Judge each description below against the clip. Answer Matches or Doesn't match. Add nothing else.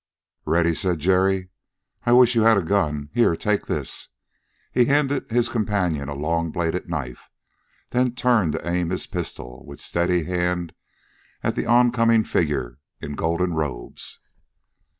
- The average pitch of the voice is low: Matches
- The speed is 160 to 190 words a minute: Doesn't match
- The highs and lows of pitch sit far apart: Matches